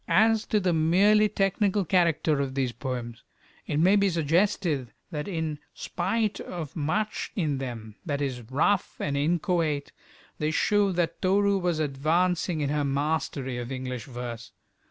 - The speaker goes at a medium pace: Yes, average, 150 wpm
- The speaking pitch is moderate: Yes, medium, 160 Hz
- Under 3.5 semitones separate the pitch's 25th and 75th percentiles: No, average, 5.3 semitones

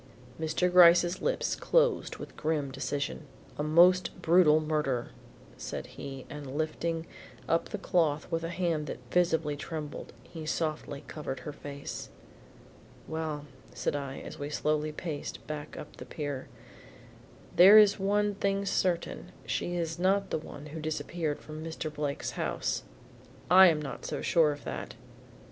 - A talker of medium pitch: Yes, medium, 155 Hz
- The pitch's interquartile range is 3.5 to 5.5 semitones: No, average, 2.9 semitones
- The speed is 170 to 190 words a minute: No, average, 150 wpm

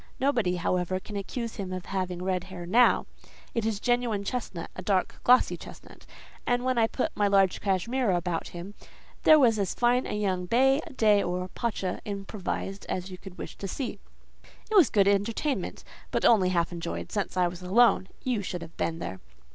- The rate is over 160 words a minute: Yes, average, 180 wpm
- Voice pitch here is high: Yes, high, 200 Hz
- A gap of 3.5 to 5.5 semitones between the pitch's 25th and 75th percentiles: Yes, average, 4.4 semitones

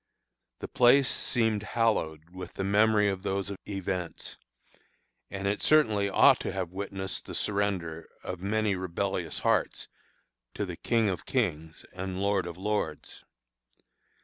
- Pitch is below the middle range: Yes, very low, 95 Hz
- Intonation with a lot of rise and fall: No, narrow, 2.4 semitones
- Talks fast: No, slow, 135 wpm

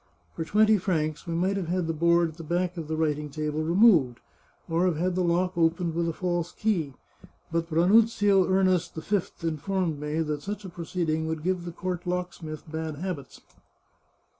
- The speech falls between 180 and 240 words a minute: Yes, average, 190 wpm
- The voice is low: No, medium, 170 Hz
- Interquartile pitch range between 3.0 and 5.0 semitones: No, narrow, 2.5 semitones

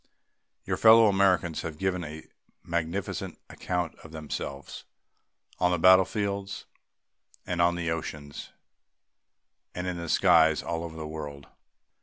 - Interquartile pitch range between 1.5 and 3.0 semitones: Yes, average, 2.7 semitones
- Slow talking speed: Yes, slow, 125 wpm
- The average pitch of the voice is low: Yes, very low, 85 Hz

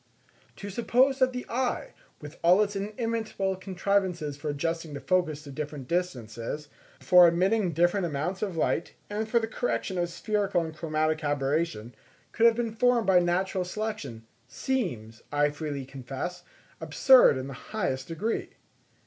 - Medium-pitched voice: Yes, medium, 175 Hz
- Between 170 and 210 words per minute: No, average, 155 wpm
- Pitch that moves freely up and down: Yes, wide, 6.1 semitones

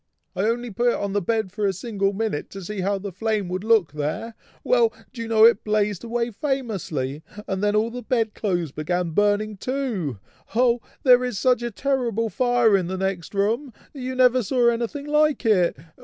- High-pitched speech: Yes, high, 220 Hz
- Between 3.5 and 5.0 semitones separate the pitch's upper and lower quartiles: Yes, average, 3.9 semitones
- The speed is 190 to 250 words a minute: Yes, average, 200 wpm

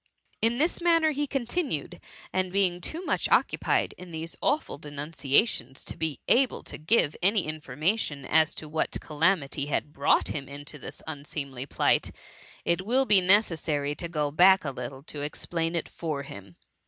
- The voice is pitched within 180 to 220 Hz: No, medium, 160 Hz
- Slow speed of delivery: No, average, 170 wpm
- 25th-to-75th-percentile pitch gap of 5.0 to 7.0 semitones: Yes, average, 5.3 semitones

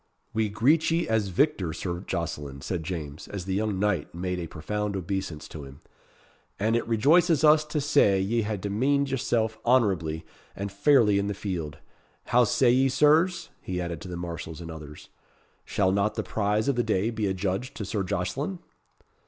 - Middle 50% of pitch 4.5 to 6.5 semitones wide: Yes, average, 5.2 semitones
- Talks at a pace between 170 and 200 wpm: Yes, average, 180 wpm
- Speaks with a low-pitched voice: Yes, low, 100 Hz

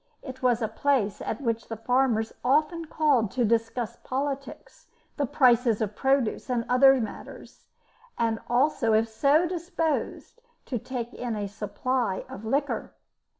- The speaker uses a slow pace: No, average, 145 wpm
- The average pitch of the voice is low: No, very high, 250 Hz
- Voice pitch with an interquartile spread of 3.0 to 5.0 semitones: Yes, average, 3.7 semitones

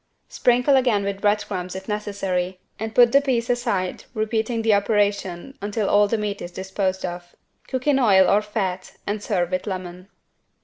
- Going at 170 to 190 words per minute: Yes, average, 175 wpm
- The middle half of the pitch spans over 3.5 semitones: No, average, 3.1 semitones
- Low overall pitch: No, high, 205 Hz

